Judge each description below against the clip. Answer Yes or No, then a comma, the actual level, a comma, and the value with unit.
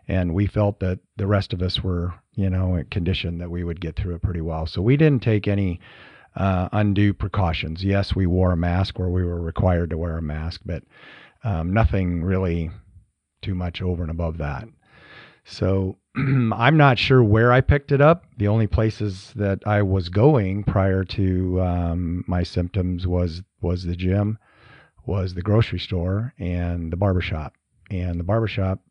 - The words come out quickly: No, average, 180 wpm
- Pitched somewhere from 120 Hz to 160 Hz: No, very low, 95 Hz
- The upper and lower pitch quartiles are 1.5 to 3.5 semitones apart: Yes, average, 2.8 semitones